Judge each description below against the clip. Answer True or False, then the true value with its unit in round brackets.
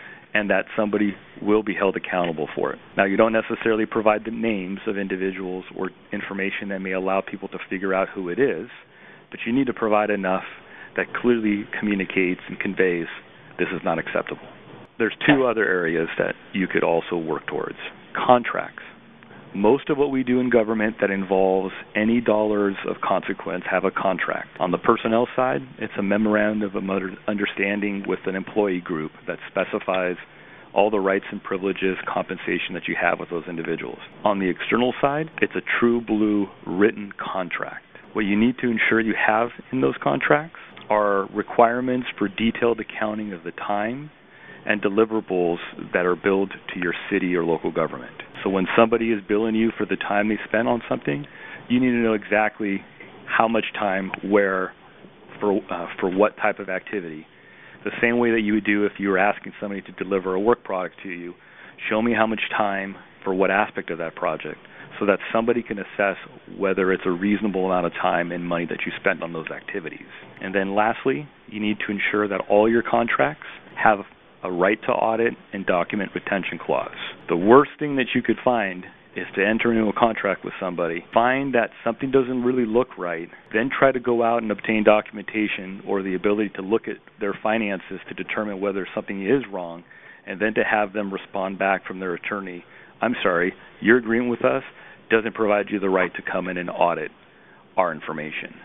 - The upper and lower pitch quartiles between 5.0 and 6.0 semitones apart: False (3.0 semitones)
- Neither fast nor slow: True (190 wpm)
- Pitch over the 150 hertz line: False (105 Hz)